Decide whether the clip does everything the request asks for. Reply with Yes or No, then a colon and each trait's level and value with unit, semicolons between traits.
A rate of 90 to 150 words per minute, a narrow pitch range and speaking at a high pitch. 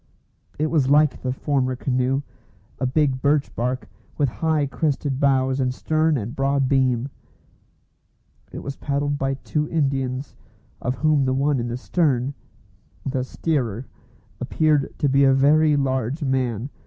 No: average, 145 wpm; narrow, 2.1 semitones; low, 135 Hz